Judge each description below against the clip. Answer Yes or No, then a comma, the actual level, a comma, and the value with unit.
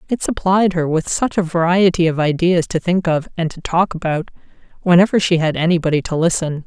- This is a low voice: No, medium, 170 Hz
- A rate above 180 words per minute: Yes, average, 200 wpm